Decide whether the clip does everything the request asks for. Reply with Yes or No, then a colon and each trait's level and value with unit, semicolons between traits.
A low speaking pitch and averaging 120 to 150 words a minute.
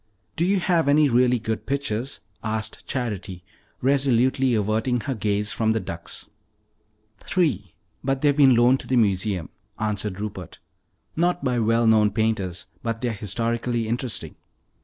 Yes: low, 115 Hz; average, 140 wpm